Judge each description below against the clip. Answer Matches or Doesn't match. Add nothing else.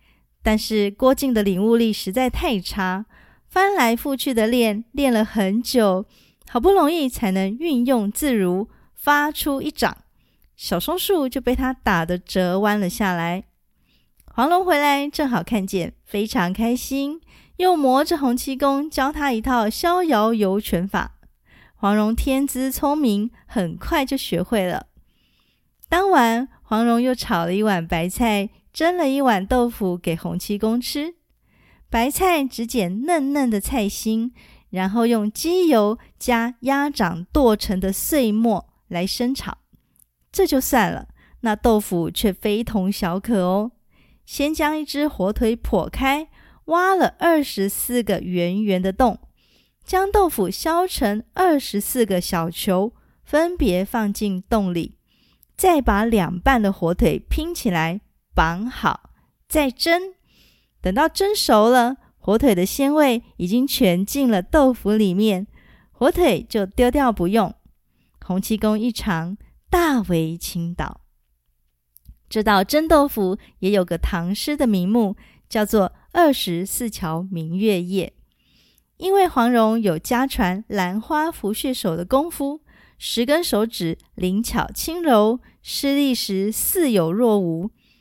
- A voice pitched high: Matches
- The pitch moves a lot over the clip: Matches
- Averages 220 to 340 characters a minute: Doesn't match